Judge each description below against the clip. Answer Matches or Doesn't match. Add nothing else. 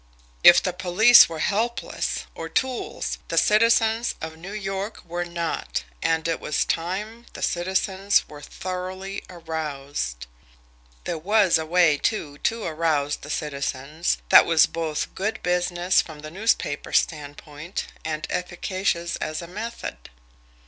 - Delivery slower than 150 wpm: Matches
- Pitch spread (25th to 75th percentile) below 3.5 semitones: Doesn't match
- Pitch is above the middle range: Doesn't match